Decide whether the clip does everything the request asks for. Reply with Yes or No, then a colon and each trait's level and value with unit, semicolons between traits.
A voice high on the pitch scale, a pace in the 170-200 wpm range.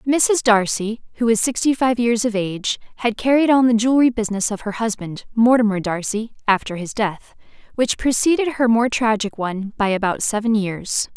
Yes: high, 225 Hz; average, 175 wpm